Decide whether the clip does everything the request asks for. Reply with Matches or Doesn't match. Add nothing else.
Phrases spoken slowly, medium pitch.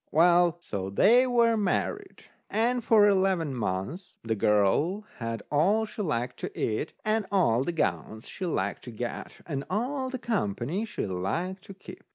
Doesn't match